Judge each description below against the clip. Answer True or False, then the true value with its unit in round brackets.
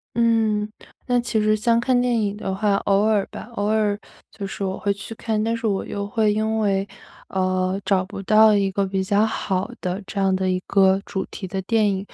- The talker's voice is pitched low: False (205 Hz)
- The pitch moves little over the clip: True (2.2 semitones)